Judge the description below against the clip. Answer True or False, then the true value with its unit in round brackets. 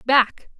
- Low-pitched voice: False (250 Hz)